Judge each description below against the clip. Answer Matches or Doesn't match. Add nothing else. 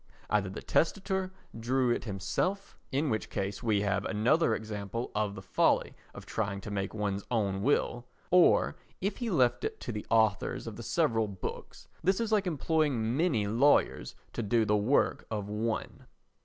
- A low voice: Matches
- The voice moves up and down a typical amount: Doesn't match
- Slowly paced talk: Doesn't match